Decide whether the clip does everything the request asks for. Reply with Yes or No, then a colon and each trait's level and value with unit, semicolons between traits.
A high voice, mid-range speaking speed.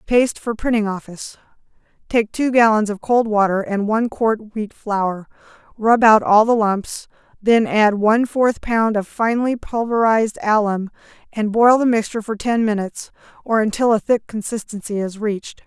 Yes: high, 215 Hz; average, 160 wpm